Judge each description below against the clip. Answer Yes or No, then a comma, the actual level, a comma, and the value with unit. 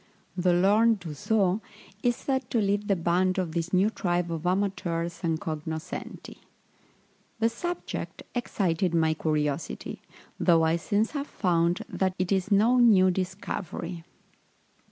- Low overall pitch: No, medium, 185 Hz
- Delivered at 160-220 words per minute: No, slow, 135 wpm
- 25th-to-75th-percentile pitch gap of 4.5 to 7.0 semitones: No, average, 3.5 semitones